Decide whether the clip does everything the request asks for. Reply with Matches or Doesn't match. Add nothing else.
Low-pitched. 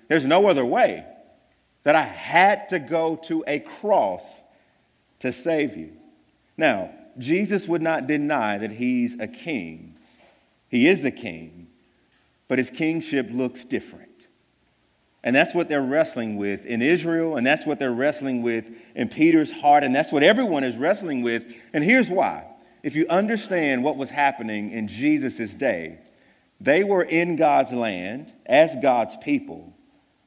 Doesn't match